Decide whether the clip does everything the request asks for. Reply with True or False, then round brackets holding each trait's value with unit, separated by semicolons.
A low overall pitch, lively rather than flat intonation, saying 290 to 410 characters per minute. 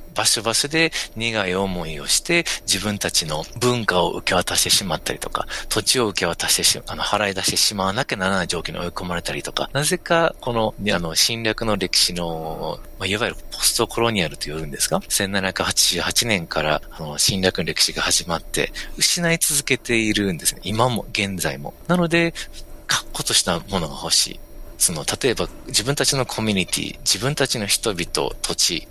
True (105 Hz; 6.1 semitones; 370 characters per minute)